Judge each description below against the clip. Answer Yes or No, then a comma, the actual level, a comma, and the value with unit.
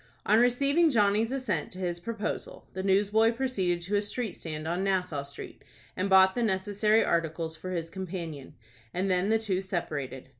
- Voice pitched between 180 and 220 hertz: Yes, high, 190 Hz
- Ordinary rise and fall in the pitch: Yes, average, 4.0 semitones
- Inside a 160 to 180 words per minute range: Yes, average, 175 wpm